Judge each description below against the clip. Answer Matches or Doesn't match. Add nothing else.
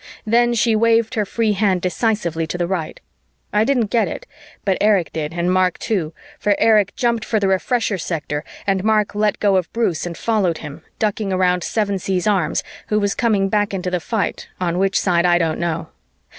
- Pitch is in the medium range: Doesn't match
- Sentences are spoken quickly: Doesn't match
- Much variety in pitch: Doesn't match